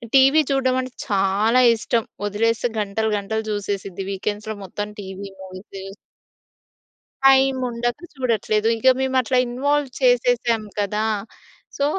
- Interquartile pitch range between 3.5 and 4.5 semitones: Yes, average, 3.9 semitones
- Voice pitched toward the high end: Yes, high, 220 Hz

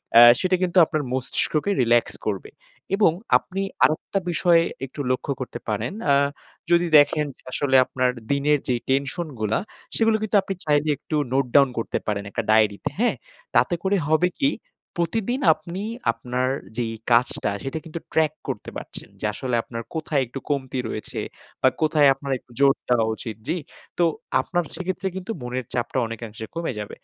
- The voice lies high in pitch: No, medium, 145 Hz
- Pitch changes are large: Yes, wide, 5.8 semitones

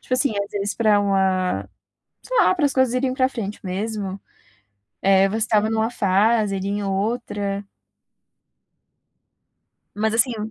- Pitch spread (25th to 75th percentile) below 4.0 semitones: Yes, average, 3.0 semitones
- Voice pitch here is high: Yes, high, 210 Hz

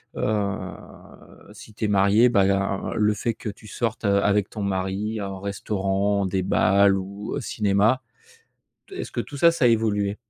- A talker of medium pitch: No, low, 100 Hz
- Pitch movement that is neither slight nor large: No, narrow, 1.8 semitones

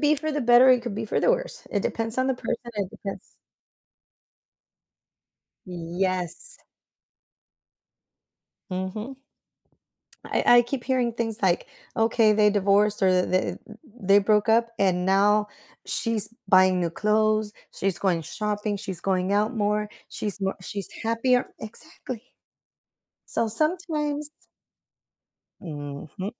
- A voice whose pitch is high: Yes, high, 210 Hz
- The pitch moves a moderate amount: Yes, average, 3.8 semitones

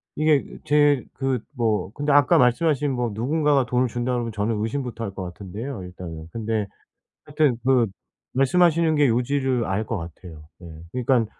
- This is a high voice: No, low, 125 Hz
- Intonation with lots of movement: No, average, 4.7 semitones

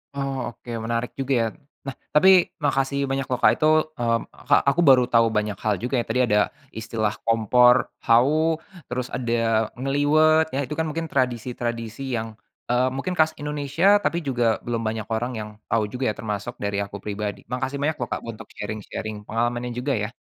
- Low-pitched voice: Yes, low, 125 Hz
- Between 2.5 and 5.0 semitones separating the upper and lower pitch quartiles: Yes, average, 3.4 semitones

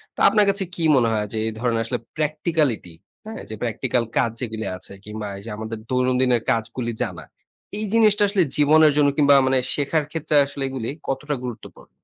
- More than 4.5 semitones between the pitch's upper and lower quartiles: Yes, average, 5.1 semitones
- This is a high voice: No, low, 130 Hz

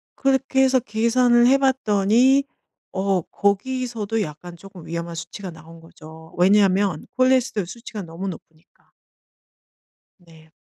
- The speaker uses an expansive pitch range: Yes, wide, 6.4 semitones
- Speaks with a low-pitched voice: No, high, 200 Hz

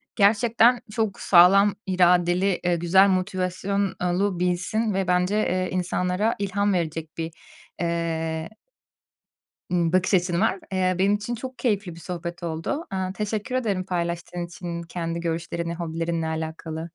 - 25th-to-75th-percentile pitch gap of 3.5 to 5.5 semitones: No, average, 2.7 semitones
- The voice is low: No, medium, 180 Hz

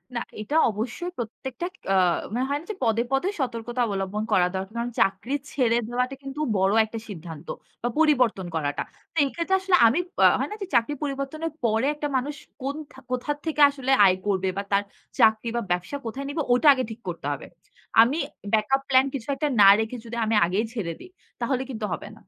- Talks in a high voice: Yes, high, 235 Hz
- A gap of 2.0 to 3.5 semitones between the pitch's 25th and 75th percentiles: No, average, 4.5 semitones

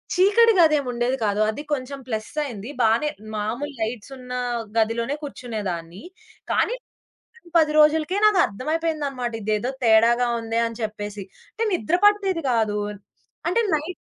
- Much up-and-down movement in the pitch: Yes, wide, 6.0 semitones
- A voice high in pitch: Yes, very high, 250 Hz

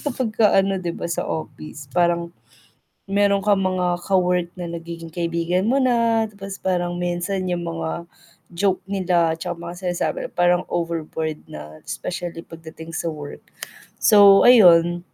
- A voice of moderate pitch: Yes, medium, 175 Hz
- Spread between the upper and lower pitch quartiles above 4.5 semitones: No, narrow, 2.6 semitones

